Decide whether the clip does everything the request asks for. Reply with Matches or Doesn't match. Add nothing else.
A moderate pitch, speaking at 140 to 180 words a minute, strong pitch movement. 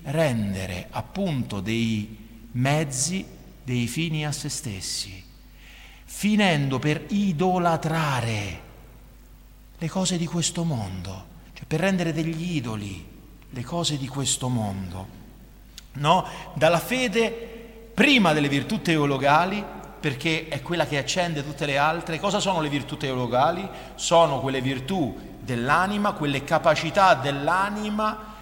Doesn't match